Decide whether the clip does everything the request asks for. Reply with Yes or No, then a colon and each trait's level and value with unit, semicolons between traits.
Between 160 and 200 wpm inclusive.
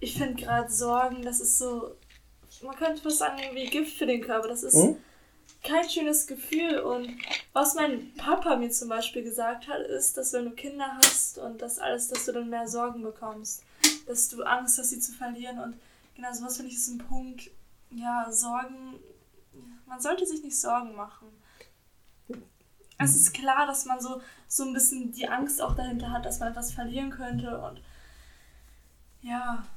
Yes: average, 180 wpm